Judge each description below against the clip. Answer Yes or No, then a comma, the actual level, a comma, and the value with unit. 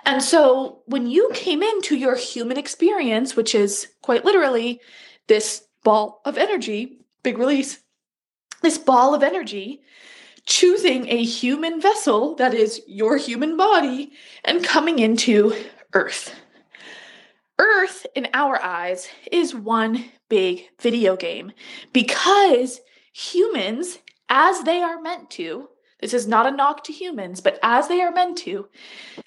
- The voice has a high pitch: Yes, very high, 270 Hz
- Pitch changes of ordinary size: No, wide, 6.7 semitones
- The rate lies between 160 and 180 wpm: No, slow, 135 wpm